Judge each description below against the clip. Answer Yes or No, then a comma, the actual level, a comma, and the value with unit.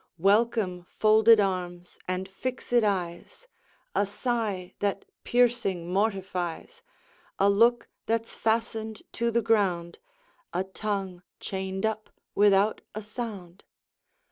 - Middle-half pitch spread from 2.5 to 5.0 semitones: Yes, average, 3.3 semitones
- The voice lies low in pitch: No, high, 205 Hz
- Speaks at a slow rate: Yes, slow, 105 wpm